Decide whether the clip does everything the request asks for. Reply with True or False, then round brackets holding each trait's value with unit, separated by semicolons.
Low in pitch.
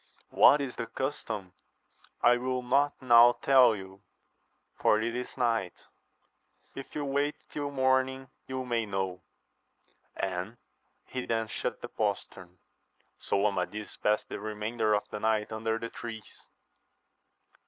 True (115 Hz)